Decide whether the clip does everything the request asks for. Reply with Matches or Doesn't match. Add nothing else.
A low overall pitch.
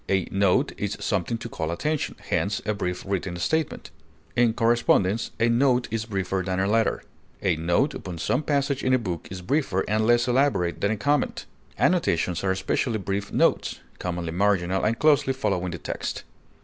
Matches